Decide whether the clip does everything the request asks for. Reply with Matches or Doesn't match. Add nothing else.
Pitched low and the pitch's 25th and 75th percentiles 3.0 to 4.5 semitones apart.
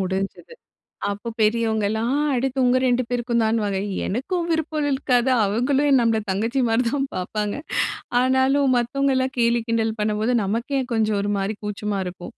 Doesn't match